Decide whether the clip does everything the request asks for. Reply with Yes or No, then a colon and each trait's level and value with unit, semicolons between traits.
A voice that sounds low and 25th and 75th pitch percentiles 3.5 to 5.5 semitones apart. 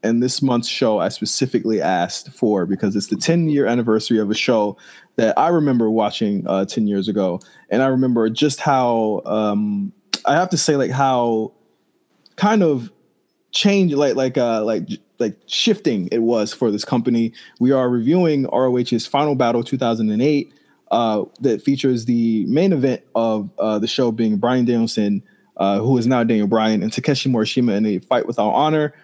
Yes: low, 120 Hz; average, 3.9 semitones